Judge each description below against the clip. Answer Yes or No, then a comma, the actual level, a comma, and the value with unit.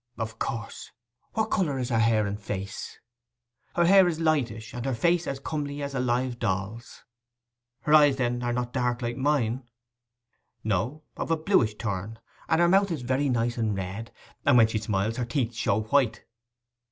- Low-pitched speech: Yes, low, 120 Hz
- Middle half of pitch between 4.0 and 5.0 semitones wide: Yes, average, 4.4 semitones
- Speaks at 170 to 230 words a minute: Yes, average, 175 wpm